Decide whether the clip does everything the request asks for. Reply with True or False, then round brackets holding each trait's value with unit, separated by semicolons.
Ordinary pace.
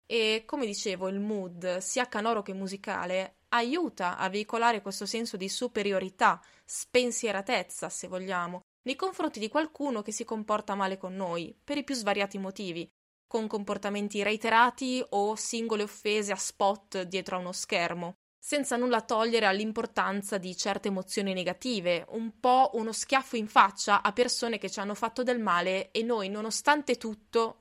True (155 wpm)